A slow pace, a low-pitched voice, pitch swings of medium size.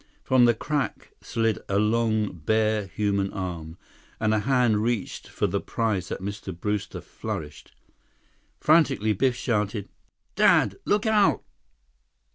Yes: slow, 125 wpm; low, 110 Hz; average, 3.4 semitones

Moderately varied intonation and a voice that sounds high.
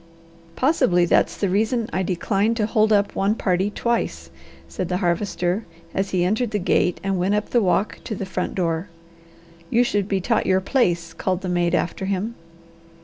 Yes: average, 3.1 semitones; high, 195 Hz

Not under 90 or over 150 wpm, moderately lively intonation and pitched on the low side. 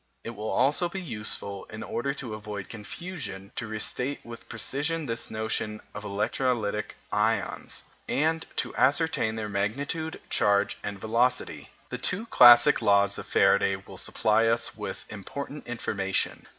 Yes: average, 140 wpm; average, 4.8 semitones; low, 115 Hz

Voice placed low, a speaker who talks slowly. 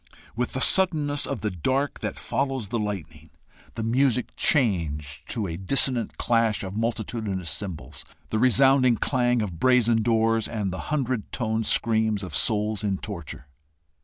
No: low, 110 Hz; average, 150 wpm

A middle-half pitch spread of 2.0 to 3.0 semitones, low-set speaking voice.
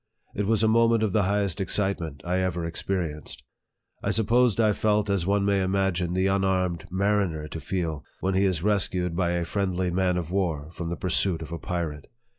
Yes: narrow, 2.6 semitones; very low, 95 Hz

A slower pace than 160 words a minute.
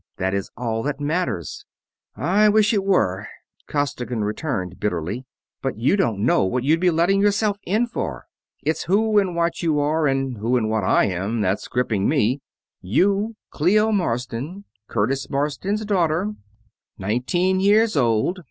Yes: average, 150 wpm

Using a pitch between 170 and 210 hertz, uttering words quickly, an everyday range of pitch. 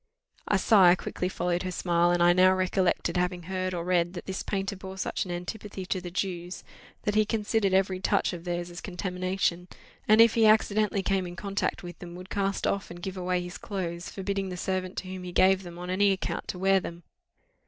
No: medium, 185 Hz; fast, 215 wpm; narrow, 1.7 semitones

